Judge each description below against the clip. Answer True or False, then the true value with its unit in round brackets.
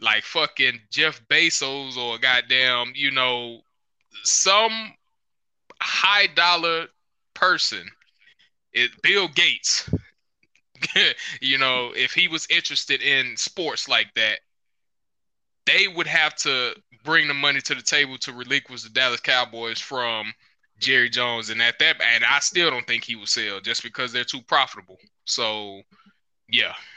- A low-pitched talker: True (125 Hz)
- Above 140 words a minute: False (135 wpm)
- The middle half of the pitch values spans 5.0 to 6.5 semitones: False (4.3 semitones)